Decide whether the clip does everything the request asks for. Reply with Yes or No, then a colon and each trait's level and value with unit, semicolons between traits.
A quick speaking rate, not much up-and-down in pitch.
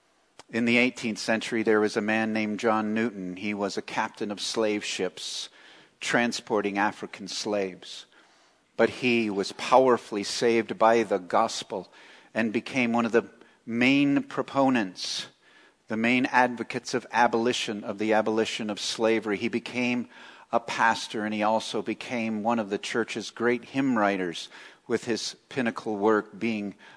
No: average, 145 wpm; narrow, 2.0 semitones